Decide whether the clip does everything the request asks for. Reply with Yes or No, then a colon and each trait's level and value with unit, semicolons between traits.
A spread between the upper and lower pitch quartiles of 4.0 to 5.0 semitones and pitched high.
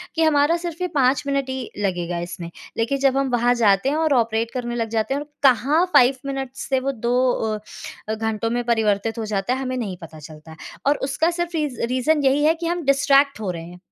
Yes: average, 4.3 semitones; very high, 255 Hz